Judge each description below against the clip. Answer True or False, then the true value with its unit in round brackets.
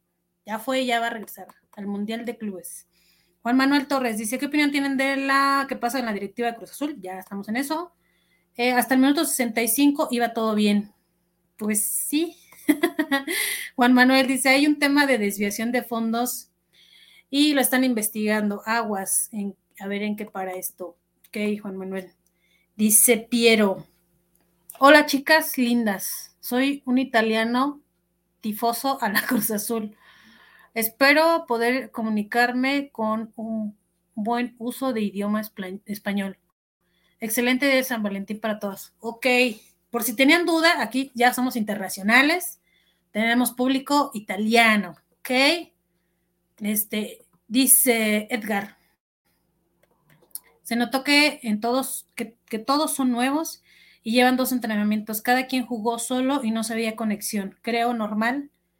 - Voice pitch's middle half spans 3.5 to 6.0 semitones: True (4.3 semitones)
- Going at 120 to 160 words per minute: True (140 wpm)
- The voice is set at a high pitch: True (230 Hz)